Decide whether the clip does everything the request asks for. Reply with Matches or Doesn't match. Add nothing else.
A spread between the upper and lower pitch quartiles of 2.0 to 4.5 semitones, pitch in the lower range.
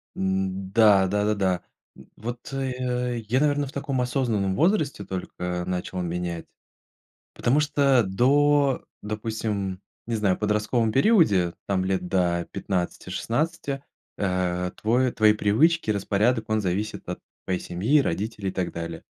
Doesn't match